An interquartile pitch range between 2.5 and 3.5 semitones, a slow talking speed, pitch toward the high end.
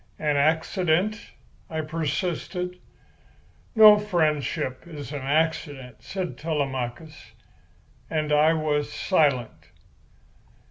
No: average, 3.0 semitones; slow, 85 wpm; medium, 155 Hz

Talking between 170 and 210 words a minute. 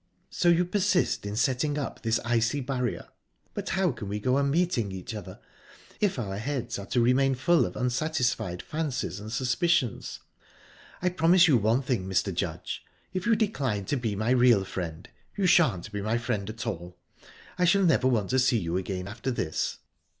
Yes: average, 180 wpm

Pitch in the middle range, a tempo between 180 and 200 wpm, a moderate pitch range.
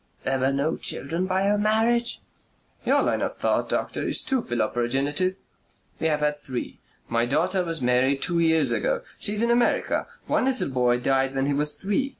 No: medium, 155 Hz; average, 185 wpm; wide, 7.3 semitones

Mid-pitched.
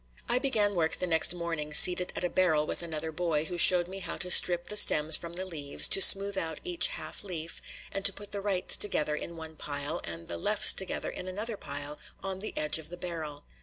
Yes: medium, 175 Hz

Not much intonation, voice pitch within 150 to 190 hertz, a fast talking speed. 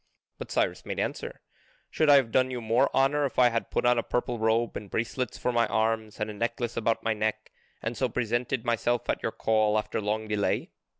No: narrow, 2.2 semitones; low, 115 Hz; fast, 220 wpm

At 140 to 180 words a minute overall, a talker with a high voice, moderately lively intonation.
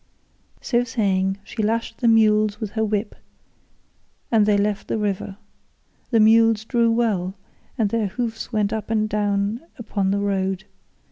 No: average, 150 wpm; high, 215 Hz; narrow, 2.0 semitones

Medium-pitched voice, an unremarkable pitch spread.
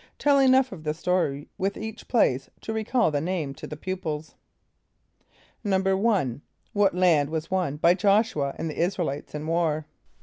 Yes: medium, 180 Hz; average, 5.0 semitones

